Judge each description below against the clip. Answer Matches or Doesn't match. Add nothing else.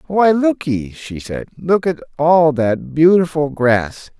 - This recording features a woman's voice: Doesn't match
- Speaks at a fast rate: Doesn't match